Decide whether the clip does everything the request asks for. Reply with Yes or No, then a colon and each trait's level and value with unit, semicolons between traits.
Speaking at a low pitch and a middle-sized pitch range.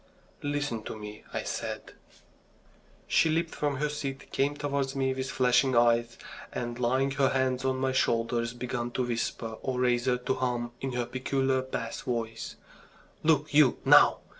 No: low, 130 Hz; narrow, 2.2 semitones